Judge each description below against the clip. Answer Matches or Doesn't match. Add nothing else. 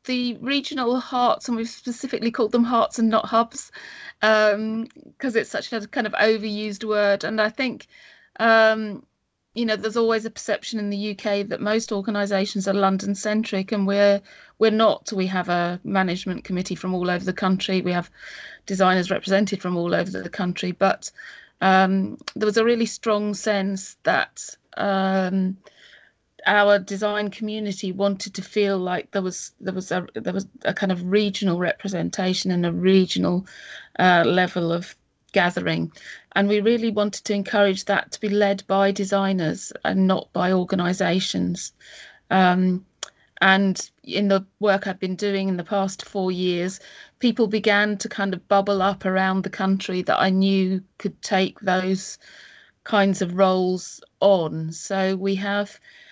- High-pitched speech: Matches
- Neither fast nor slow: Matches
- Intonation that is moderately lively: Doesn't match